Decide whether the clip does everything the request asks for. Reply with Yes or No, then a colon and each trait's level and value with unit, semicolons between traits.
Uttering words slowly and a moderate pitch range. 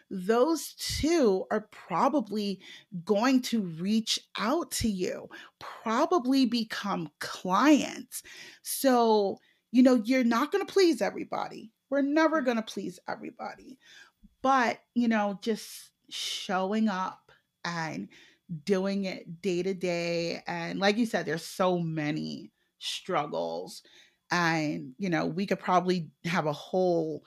No: slow, 125 wpm; wide, 6.0 semitones